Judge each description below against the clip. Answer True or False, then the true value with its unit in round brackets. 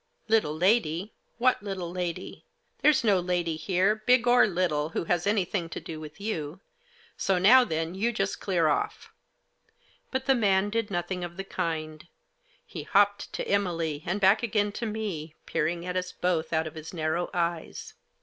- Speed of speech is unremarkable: True (175 wpm)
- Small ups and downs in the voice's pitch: False (3.9 semitones)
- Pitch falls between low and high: True (180 Hz)